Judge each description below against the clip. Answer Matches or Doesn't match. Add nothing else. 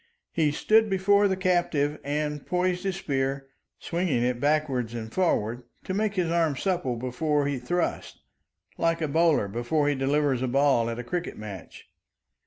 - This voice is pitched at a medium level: Matches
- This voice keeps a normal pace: Matches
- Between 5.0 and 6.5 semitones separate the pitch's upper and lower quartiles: Matches